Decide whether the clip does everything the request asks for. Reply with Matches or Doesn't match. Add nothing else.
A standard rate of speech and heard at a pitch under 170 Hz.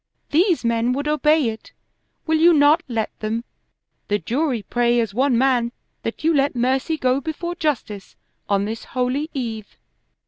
Doesn't match